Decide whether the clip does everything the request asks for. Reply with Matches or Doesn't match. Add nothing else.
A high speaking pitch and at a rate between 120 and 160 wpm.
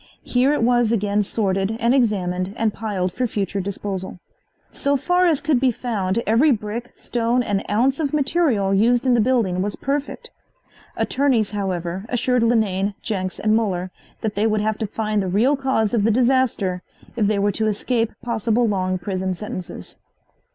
Doesn't match